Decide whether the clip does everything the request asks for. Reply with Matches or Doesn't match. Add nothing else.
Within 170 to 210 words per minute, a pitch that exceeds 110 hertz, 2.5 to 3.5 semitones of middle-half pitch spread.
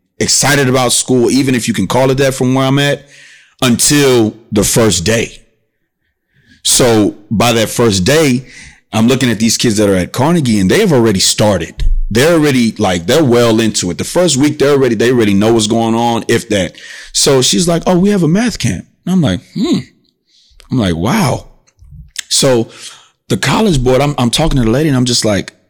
Doesn't match